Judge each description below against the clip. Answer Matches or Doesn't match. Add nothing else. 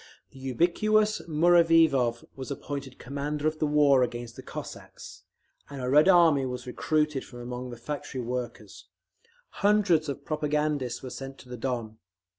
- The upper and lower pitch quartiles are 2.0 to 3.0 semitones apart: Doesn't match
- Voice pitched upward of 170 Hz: Doesn't match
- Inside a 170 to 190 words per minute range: Doesn't match